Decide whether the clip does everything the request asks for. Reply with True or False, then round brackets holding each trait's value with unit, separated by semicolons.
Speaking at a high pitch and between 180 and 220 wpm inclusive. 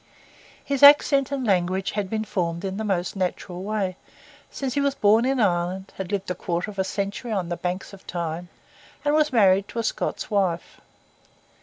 True (195 Hz; 190 wpm)